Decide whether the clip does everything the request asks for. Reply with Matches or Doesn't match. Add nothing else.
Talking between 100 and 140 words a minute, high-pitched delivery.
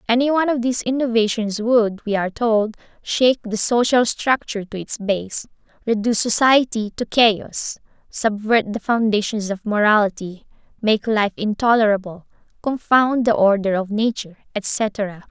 Matches